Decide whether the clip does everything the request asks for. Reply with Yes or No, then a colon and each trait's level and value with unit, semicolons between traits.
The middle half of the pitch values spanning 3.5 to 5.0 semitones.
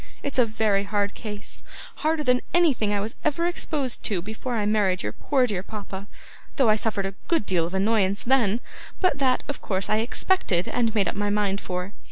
Yes: average, 4.3 semitones